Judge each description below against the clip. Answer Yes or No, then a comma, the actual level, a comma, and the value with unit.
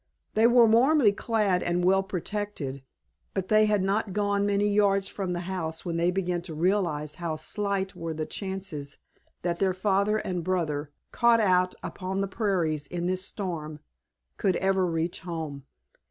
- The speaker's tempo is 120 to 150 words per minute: No, average, 165 wpm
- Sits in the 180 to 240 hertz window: Yes, medium, 185 Hz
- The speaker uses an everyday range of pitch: Yes, average, 3.0 semitones